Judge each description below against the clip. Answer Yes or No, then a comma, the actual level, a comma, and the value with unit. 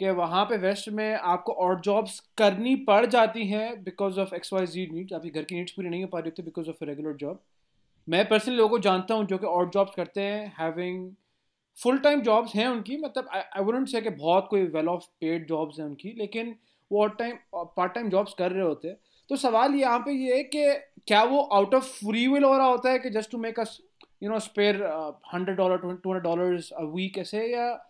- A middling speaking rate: No, fast, 230 wpm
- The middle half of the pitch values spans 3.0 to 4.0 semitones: No, average, 4.4 semitones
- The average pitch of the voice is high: Yes, high, 200 Hz